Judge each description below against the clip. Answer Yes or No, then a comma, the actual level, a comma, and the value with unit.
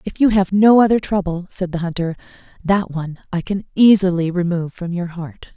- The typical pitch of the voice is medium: Yes, medium, 180 Hz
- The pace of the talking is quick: No, average, 195 wpm